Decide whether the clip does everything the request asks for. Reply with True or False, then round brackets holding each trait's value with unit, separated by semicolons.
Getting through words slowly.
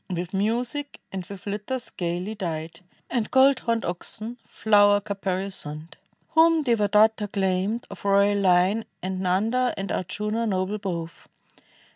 True (125 wpm)